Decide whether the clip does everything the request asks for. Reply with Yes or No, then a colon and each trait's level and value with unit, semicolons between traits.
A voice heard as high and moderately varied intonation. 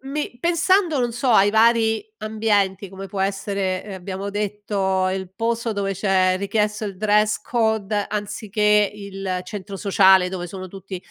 No: high, 205 Hz; narrow, 2.3 semitones